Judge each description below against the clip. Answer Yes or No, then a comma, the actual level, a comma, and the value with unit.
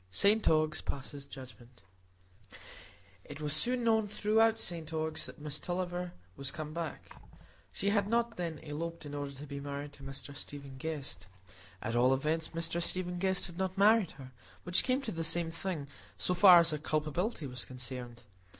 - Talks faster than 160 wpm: Yes, average, 170 wpm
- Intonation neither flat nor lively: Yes, average, 4.5 semitones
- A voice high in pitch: No, medium, 160 Hz